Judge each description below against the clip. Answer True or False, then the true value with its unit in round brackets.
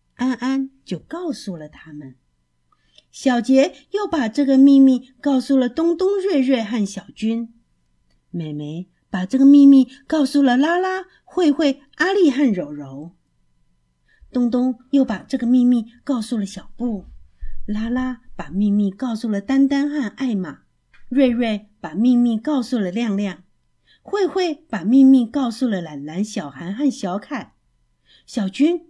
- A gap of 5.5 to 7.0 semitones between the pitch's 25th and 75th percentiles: True (6.3 semitones)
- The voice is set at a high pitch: True (245 Hz)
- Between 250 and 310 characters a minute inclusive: False (205 characters per minute)